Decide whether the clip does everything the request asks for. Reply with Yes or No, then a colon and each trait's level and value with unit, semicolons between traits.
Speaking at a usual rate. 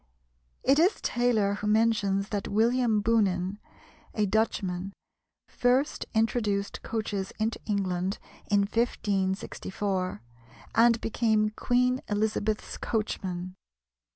No: slow, 95 wpm